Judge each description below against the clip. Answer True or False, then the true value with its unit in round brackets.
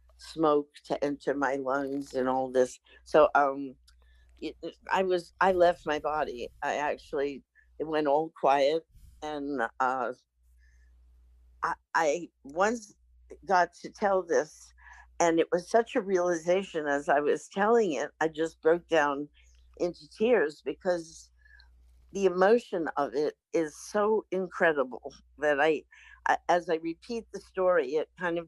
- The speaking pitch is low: False (160 Hz)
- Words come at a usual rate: True (145 wpm)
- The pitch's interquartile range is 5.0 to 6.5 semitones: True (5.4 semitones)